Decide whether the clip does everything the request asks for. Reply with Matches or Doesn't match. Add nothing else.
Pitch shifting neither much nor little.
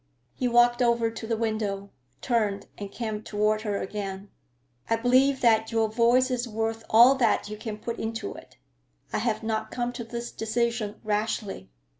Doesn't match